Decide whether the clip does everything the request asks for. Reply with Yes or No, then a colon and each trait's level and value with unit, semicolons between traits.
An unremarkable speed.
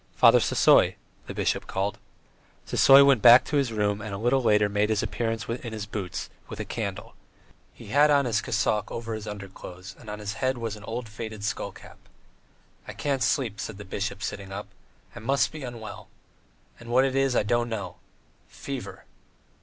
Yes: average, 190 wpm